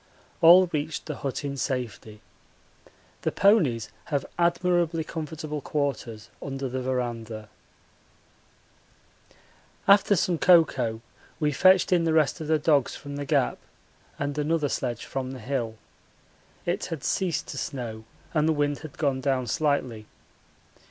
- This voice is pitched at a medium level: Yes, medium, 145 Hz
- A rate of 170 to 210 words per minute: No, slow, 135 wpm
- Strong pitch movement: No, average, 4.0 semitones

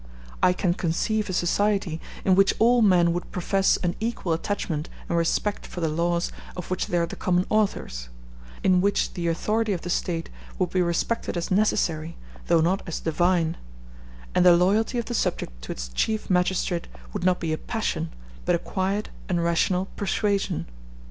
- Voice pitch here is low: No, medium, 180 Hz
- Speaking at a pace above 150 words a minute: Yes, average, 180 wpm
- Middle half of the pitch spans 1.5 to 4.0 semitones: Yes, average, 2.9 semitones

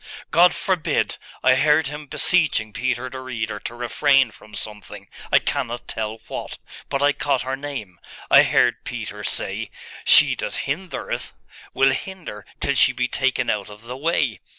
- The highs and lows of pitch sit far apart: No, average, 4.6 semitones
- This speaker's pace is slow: No, average, 160 wpm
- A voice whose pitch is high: No, low, 130 Hz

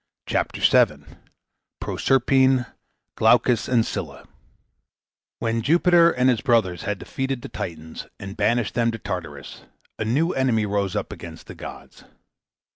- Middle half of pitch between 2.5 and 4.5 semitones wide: No, average, 4.9 semitones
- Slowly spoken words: Yes, slow, 130 wpm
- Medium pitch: No, low, 115 Hz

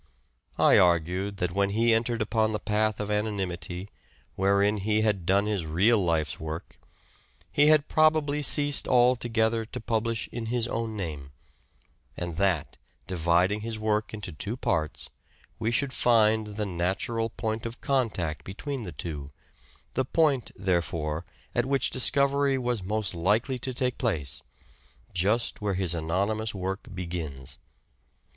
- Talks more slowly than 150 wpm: Yes, average, 140 wpm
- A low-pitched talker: Yes, low, 105 Hz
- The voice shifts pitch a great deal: No, average, 4.7 semitones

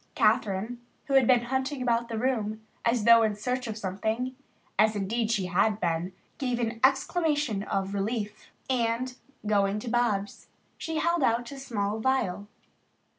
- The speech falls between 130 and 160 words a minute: Yes, average, 155 wpm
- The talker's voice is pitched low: No, high, 230 Hz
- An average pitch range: Yes, average, 3.6 semitones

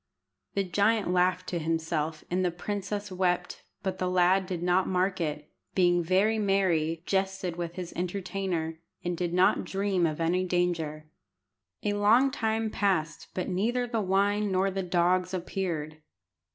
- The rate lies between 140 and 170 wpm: Yes, average, 150 wpm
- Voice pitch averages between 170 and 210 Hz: Yes, medium, 185 Hz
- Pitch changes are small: Yes, narrow, 2.2 semitones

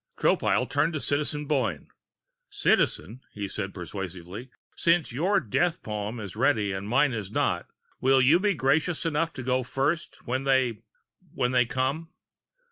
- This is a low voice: Yes, low, 130 Hz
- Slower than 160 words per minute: Yes, average, 150 wpm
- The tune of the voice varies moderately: No, wide, 5.9 semitones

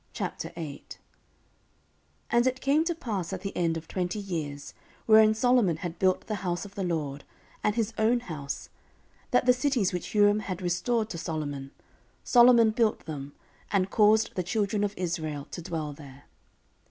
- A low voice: No, high, 190 Hz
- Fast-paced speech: No, average, 165 wpm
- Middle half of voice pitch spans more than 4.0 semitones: Yes, average, 5.2 semitones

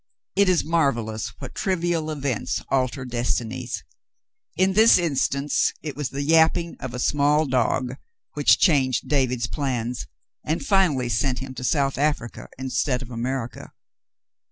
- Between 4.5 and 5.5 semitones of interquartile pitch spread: No, average, 3.8 semitones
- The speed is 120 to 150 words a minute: Yes, slow, 135 wpm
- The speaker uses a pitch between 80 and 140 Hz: Yes, low, 135 Hz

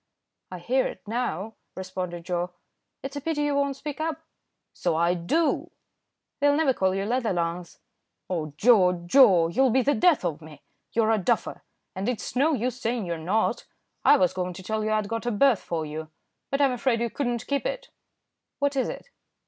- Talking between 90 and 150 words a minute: No, average, 200 wpm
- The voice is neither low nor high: No, high, 220 Hz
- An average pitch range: No, wide, 7.1 semitones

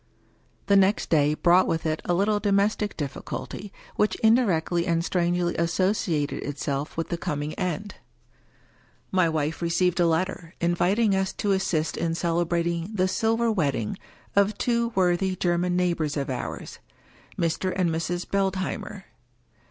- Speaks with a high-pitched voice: No, medium, 175 Hz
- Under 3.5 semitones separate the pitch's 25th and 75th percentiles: Yes, average, 2.9 semitones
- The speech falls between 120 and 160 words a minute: Yes, average, 150 wpm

